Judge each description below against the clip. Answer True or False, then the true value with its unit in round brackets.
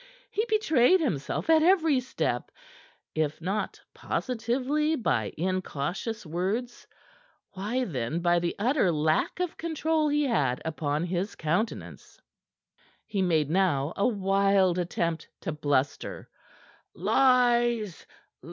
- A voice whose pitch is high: True (195 Hz)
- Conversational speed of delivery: False (110 wpm)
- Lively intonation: True (7.6 semitones)